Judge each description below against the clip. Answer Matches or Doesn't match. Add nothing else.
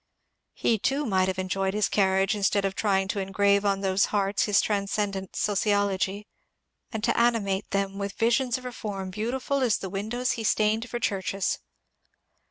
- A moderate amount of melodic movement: Doesn't match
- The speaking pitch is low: Doesn't match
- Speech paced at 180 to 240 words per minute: Doesn't match